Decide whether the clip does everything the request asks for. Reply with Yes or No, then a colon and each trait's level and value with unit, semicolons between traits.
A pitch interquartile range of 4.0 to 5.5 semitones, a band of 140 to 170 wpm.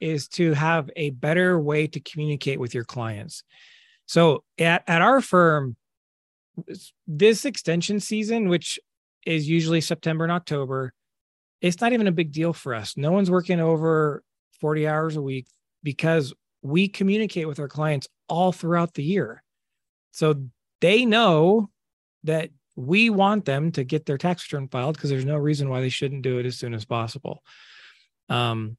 Yes: average, 4.3 semitones; average, 165 wpm